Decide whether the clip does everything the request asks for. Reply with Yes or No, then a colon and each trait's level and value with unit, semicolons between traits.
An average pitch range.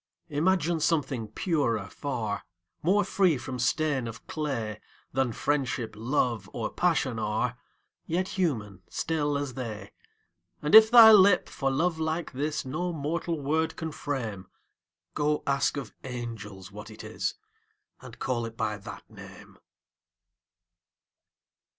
No: wide, 5.8 semitones